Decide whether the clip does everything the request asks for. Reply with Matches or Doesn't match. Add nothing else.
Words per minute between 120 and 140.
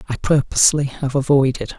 Matches